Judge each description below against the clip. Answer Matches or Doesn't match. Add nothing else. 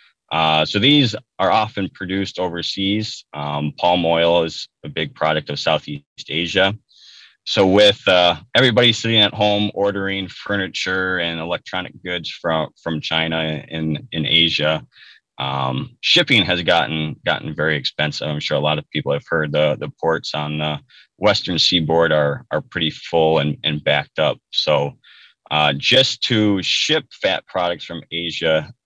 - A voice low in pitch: Matches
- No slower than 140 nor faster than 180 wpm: Matches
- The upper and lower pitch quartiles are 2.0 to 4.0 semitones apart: Doesn't match